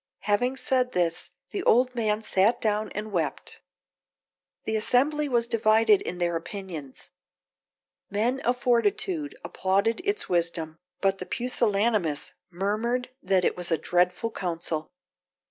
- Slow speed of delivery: Yes, slow, 130 wpm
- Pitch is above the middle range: Yes, high, 210 Hz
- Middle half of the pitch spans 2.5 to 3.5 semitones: No, average, 5.3 semitones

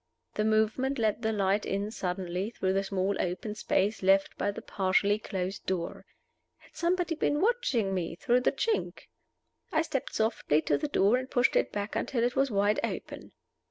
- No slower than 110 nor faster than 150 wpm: No, average, 180 wpm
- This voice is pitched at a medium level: No, high, 210 Hz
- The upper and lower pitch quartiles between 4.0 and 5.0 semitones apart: Yes, average, 4.6 semitones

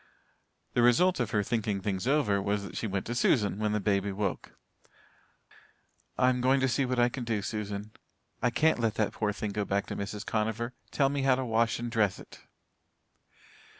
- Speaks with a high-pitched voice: No, low, 110 Hz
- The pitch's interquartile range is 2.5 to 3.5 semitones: Yes, average, 3.2 semitones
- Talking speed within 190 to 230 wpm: Yes, average, 200 wpm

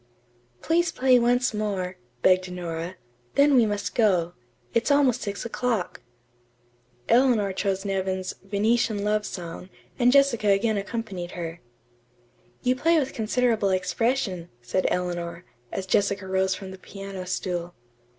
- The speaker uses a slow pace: Yes, slow, 130 wpm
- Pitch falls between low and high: No, high, 200 Hz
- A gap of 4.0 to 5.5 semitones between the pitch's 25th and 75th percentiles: Yes, average, 4.4 semitones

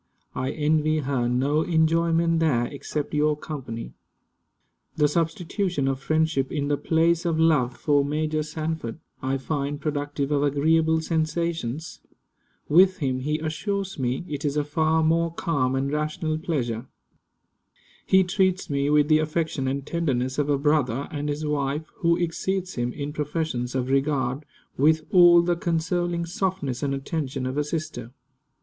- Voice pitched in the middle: Yes, medium, 150 Hz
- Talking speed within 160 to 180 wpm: No, average, 150 wpm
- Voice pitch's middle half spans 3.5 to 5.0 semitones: No, average, 2.8 semitones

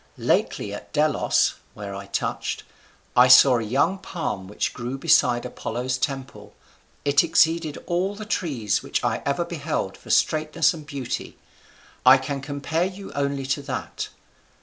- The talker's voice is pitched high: No, medium, 140 Hz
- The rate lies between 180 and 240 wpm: No, average, 150 wpm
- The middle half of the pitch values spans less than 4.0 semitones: No, average, 4.4 semitones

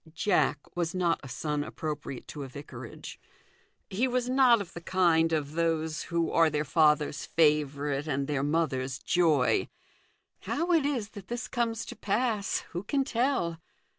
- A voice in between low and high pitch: Yes, medium, 165 Hz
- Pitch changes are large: Yes, wide, 6.1 semitones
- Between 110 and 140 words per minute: No, average, 160 wpm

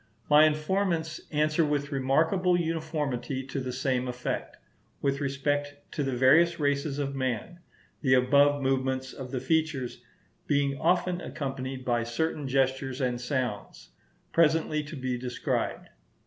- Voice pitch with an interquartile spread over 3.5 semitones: No, average, 2.9 semitones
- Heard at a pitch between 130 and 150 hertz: Yes, medium, 140 Hz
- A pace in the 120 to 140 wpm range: Yes, slow, 135 wpm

